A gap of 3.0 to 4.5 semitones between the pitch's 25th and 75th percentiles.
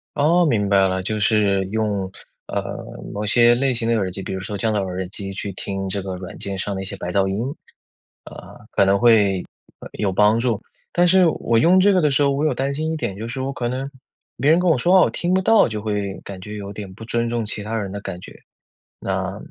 No: wide, 5.4 semitones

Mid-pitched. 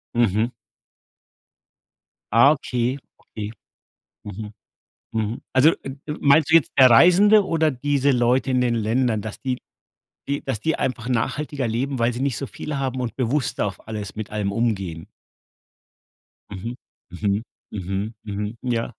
No: low, 120 Hz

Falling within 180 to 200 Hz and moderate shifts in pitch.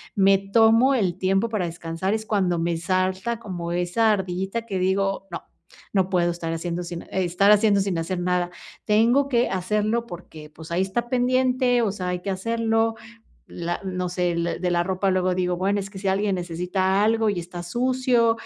Yes: high, 190 Hz; average, 3.8 semitones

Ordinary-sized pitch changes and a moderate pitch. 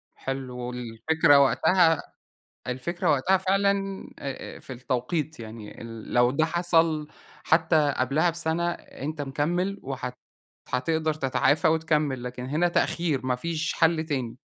Yes: average, 4.5 semitones; medium, 155 Hz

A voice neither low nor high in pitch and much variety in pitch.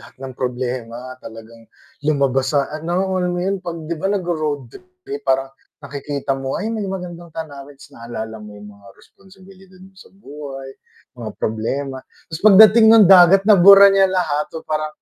Yes: medium, 150 Hz; wide, 5.9 semitones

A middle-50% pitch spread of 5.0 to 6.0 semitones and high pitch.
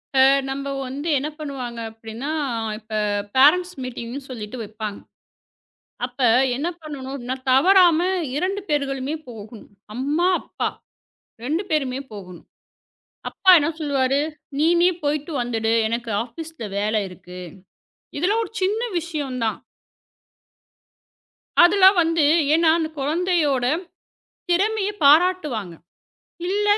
Yes: wide, 5.6 semitones; very high, 280 Hz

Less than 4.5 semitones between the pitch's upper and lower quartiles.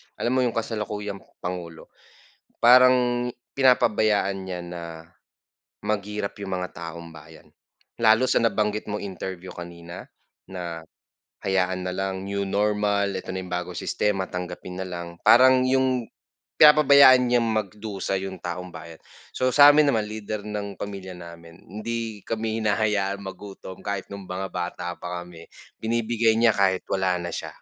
Yes: average, 3.6 semitones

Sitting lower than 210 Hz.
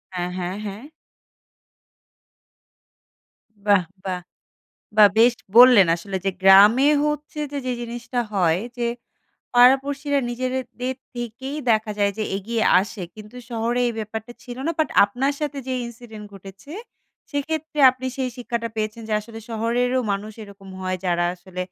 No: high, 230 Hz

